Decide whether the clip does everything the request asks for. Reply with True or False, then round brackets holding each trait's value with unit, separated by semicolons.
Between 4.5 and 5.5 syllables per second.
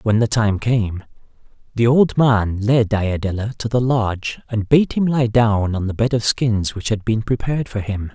True (4.7 syllables/s)